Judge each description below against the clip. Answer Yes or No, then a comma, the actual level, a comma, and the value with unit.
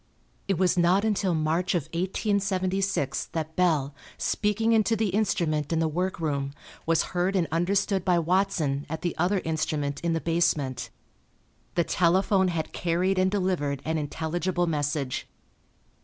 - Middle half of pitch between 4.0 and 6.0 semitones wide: No, average, 3.3 semitones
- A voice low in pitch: No, medium, 175 Hz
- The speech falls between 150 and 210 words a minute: No, average, 140 wpm